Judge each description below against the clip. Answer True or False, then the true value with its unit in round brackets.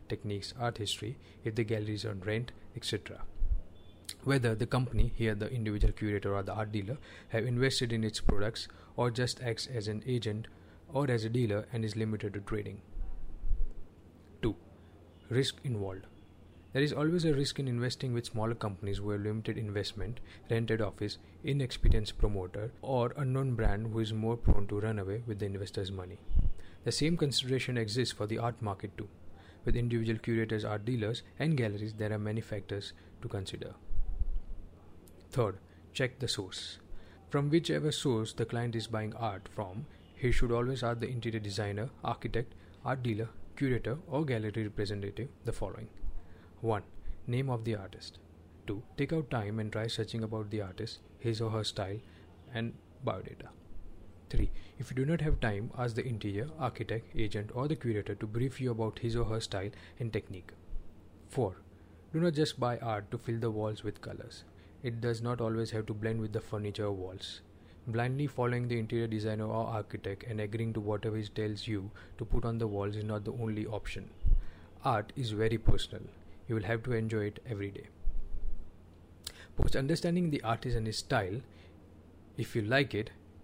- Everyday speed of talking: True (175 wpm)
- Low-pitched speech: True (110 Hz)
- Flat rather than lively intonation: False (3.2 semitones)